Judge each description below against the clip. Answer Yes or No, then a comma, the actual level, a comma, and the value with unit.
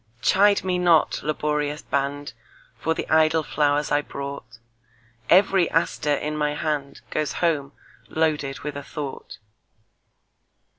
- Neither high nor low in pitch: Yes, medium, 150 Hz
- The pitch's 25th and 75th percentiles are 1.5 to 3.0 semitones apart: Yes, narrow, 2.4 semitones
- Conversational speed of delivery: No, slow, 105 wpm